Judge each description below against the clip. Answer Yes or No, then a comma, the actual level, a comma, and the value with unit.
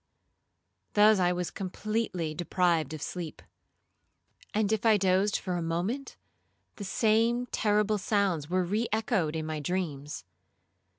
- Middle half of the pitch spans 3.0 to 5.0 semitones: Yes, average, 4.1 semitones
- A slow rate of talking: Yes, slow, 130 wpm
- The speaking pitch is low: No, medium, 185 Hz